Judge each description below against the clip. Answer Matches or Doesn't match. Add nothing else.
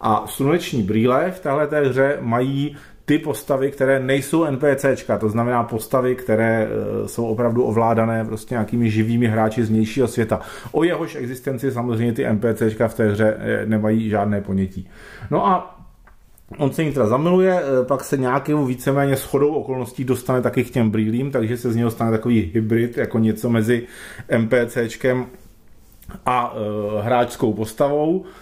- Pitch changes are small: Doesn't match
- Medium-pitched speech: Doesn't match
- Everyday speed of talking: Matches